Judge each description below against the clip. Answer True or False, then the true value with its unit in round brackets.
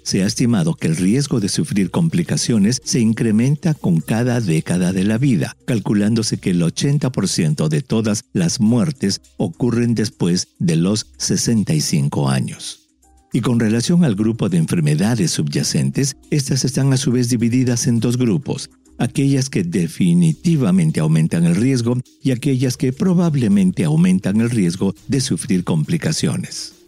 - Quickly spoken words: False (145 wpm)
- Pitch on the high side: False (140 Hz)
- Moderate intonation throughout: False (6.1 semitones)